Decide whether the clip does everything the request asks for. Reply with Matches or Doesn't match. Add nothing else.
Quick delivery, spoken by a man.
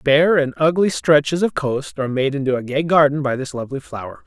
Matches